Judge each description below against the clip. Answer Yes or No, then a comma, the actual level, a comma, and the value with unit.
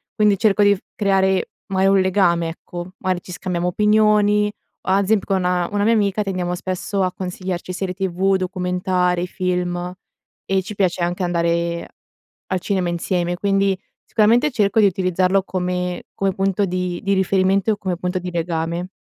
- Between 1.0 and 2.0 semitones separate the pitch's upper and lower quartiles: Yes, narrow, 1.7 semitones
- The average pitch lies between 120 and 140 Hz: No, medium, 185 Hz